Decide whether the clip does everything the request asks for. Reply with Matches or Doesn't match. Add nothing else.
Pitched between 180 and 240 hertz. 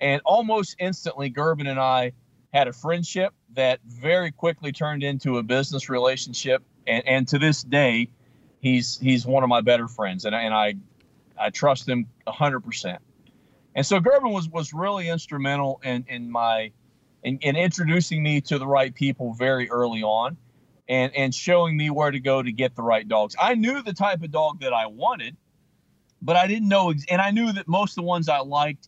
Doesn't match